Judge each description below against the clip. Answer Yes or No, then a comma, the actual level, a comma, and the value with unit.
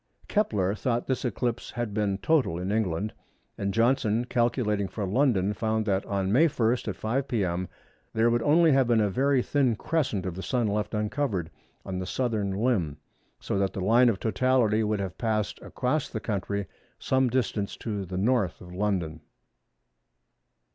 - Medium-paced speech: Yes, average, 170 wpm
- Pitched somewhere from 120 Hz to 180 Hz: No, low, 110 Hz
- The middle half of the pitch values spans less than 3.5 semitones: No, average, 4.0 semitones